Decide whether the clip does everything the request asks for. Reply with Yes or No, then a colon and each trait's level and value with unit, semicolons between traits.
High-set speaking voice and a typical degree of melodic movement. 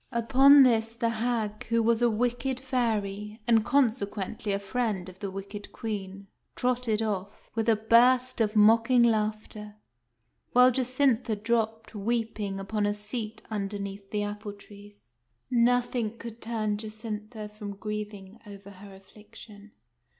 No: high, 215 Hz; narrow, 2.3 semitones